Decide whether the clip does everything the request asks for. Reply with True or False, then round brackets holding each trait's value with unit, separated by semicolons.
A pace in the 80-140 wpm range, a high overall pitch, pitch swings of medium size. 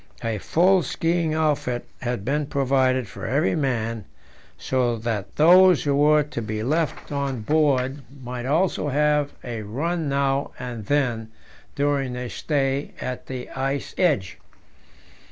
False (135 wpm; 135 Hz; 3.5 semitones)